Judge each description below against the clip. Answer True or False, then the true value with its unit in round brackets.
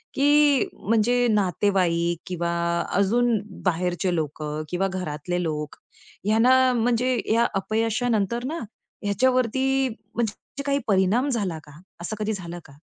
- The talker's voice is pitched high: True (210 Hz)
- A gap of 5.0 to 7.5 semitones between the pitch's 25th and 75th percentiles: True (5.5 semitones)